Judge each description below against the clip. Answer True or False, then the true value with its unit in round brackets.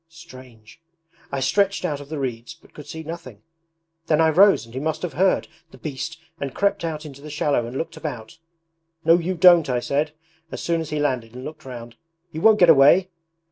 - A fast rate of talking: True (210 wpm)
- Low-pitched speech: False (150 Hz)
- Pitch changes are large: False (4.2 semitones)